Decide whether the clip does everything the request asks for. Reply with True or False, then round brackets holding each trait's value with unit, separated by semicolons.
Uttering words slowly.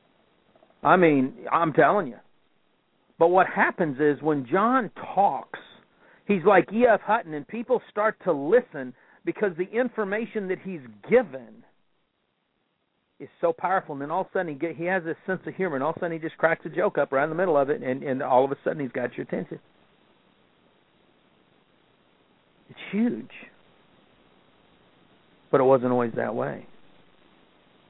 False (170 wpm)